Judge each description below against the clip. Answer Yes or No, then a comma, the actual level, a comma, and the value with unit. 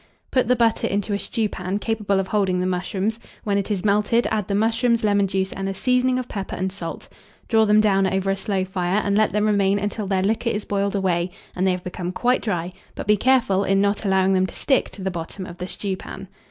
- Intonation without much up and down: Yes, narrow, 2.2 semitones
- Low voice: No, high, 200 Hz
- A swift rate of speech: Yes, fast, 235 wpm